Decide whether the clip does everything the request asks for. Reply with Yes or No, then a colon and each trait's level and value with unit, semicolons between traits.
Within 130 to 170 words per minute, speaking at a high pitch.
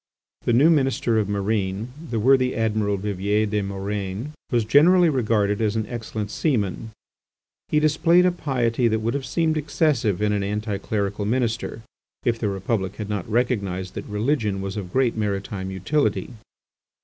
No: average, 160 wpm; low, 110 Hz